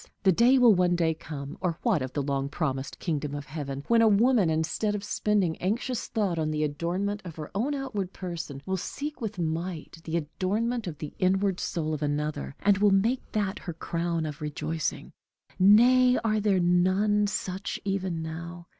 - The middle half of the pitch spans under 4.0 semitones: No, average, 4.8 semitones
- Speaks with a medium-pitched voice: Yes, medium, 180 Hz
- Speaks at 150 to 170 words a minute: No, average, 185 wpm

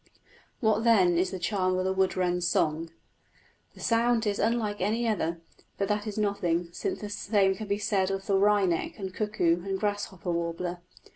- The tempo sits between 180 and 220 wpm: Yes, average, 185 wpm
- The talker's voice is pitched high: Yes, high, 195 Hz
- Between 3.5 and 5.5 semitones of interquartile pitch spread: No, average, 2.9 semitones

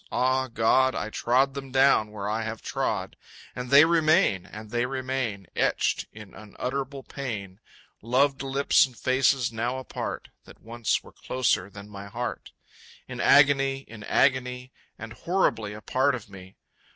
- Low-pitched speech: Yes, low, 125 Hz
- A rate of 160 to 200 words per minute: No, average, 150 wpm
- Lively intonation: No, average, 3.8 semitones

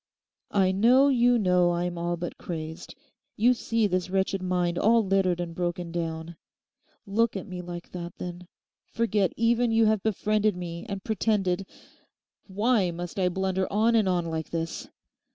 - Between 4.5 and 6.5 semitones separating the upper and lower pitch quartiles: No, average, 3.5 semitones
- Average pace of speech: Yes, average, 155 wpm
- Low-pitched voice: No, medium, 185 Hz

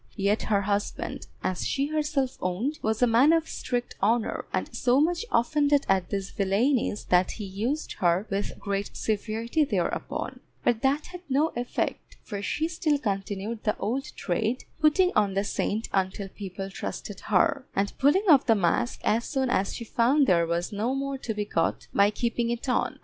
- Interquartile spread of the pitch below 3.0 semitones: No, wide, 5.5 semitones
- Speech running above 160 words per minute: Yes, average, 180 wpm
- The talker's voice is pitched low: No, high, 225 Hz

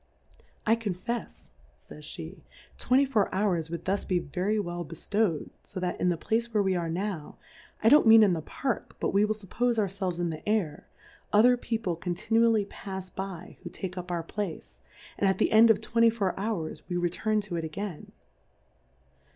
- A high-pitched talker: Yes, high, 195 Hz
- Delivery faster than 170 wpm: Yes, average, 190 wpm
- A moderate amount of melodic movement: Yes, average, 4.0 semitones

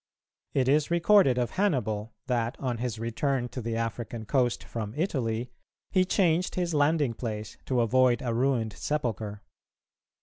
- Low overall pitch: Yes, low, 125 Hz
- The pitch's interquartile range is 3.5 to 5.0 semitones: Yes, average, 4.2 semitones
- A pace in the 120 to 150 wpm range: Yes, average, 145 wpm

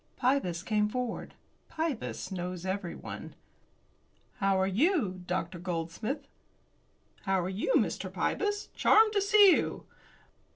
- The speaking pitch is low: No, high, 210 Hz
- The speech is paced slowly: Yes, slow, 115 wpm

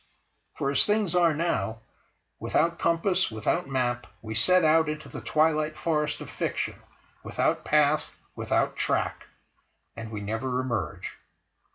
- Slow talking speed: Yes, slow, 130 wpm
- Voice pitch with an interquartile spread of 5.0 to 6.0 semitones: Yes, wide, 5.4 semitones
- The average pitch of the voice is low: No, medium, 150 Hz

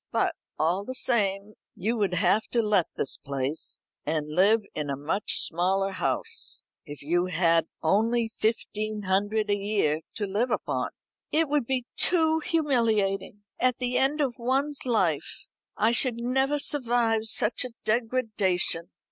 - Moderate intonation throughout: Yes, average, 5.0 semitones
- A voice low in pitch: No, high, 215 Hz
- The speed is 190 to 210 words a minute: No, average, 150 wpm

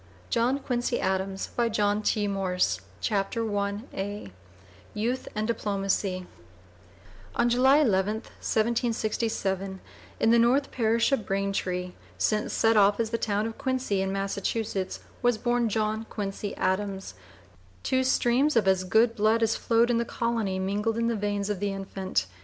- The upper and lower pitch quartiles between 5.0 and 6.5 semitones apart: No, average, 3.0 semitones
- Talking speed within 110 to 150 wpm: Yes, average, 140 wpm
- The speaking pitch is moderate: No, high, 215 Hz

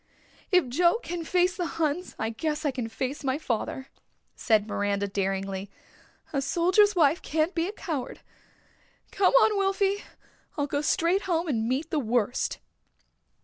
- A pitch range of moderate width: No, wide, 6.7 semitones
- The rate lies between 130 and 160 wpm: Yes, average, 145 wpm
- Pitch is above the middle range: Yes, very high, 300 Hz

